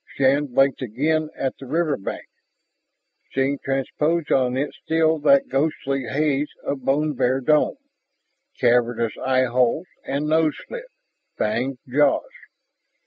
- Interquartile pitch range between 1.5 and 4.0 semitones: Yes, average, 2.8 semitones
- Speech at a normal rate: No, slow, 115 wpm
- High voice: No, low, 135 Hz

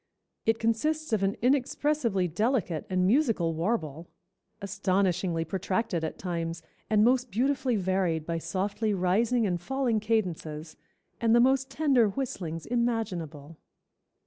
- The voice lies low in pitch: No, high, 200 Hz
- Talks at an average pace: No, slow, 120 wpm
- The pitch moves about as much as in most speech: No, wide, 5.7 semitones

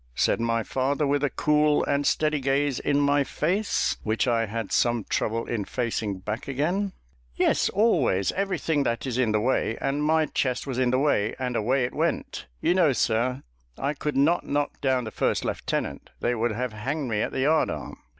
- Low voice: Yes, low, 130 Hz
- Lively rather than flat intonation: No, average, 4.0 semitones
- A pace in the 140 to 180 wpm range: No, average, 200 wpm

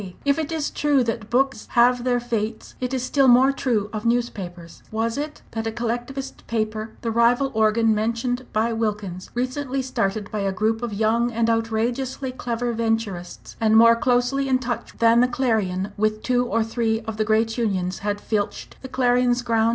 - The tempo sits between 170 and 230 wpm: Yes, average, 180 wpm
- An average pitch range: No, narrow, 2.3 semitones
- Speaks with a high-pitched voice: Yes, high, 230 Hz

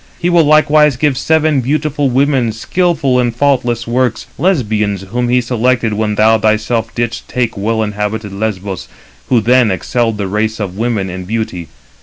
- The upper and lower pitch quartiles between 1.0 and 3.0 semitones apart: No, average, 3.7 semitones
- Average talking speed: Yes, average, 160 wpm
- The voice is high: No, low, 115 Hz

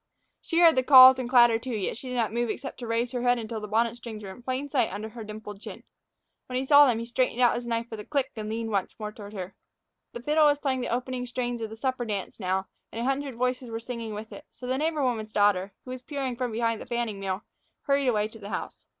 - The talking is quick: Yes, fast, 270 wpm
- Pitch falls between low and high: No, high, 235 Hz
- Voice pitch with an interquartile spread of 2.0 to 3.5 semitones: Yes, average, 2.9 semitones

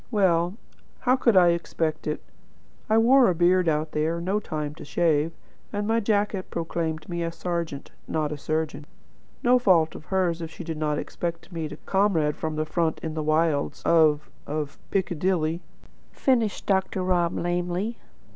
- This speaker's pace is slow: No, average, 170 wpm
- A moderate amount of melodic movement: Yes, average, 3.4 semitones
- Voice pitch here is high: No, medium, 170 Hz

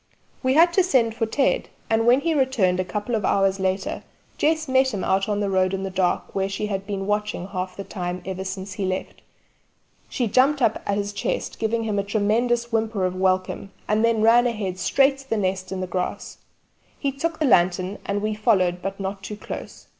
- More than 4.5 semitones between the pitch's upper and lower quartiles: No, average, 3.8 semitones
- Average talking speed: No, fast, 215 wpm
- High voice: Yes, high, 205 Hz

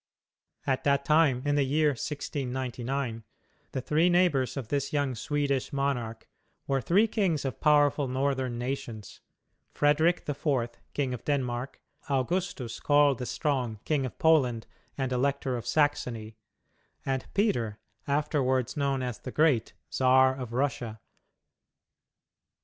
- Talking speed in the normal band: No, slow, 130 wpm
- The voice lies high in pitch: No, low, 135 Hz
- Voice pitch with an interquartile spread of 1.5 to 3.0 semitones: Yes, average, 2.7 semitones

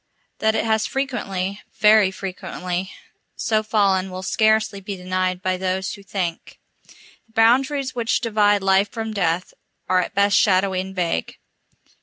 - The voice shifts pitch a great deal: No, average, 2.8 semitones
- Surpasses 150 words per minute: No, average, 145 wpm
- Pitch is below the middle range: No, high, 195 Hz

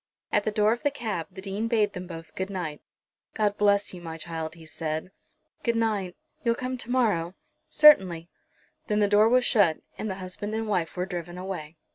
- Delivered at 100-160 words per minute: No, average, 200 wpm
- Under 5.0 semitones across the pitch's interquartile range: Yes, average, 4.1 semitones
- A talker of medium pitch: No, high, 195 Hz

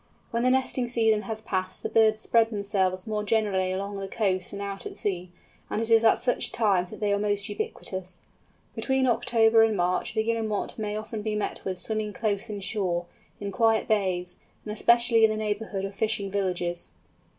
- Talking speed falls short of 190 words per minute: No, average, 195 wpm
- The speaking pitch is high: Yes, high, 210 Hz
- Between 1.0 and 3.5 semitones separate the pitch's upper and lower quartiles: Yes, narrow, 2.4 semitones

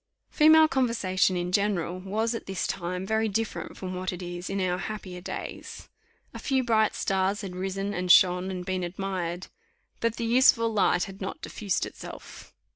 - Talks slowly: No, average, 175 wpm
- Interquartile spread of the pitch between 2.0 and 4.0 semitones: Yes, average, 3.2 semitones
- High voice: Yes, high, 195 Hz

